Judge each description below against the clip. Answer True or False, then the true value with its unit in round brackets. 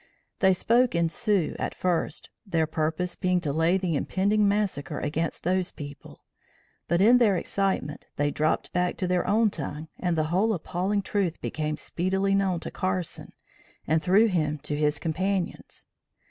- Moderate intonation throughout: True (3.7 semitones)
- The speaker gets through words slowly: False (160 wpm)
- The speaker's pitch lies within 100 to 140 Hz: False (180 Hz)